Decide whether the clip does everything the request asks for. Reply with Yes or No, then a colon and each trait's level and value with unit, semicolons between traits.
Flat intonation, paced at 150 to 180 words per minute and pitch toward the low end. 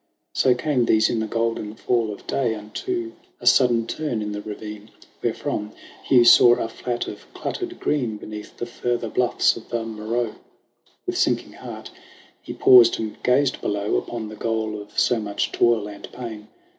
Yes: narrow, 2.3 semitones; average, 170 wpm; low, 115 Hz